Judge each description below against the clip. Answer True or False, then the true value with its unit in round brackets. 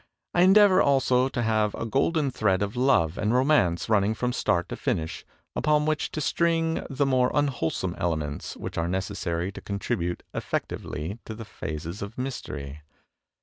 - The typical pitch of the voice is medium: False (110 Hz)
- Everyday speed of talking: True (165 wpm)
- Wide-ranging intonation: True (7.5 semitones)